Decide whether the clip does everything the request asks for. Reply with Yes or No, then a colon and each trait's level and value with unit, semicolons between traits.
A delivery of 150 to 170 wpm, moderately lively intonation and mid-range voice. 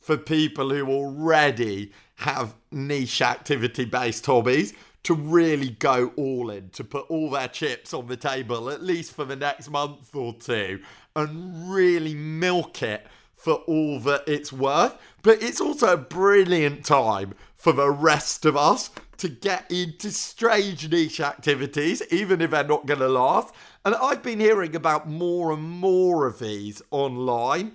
Yes: average, 160 wpm; average, 4.1 semitones; medium, 150 Hz